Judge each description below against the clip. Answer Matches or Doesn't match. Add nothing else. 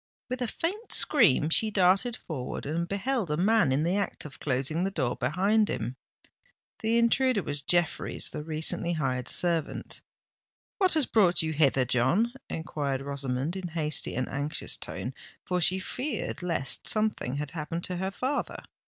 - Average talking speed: Matches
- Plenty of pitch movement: Matches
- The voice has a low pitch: Doesn't match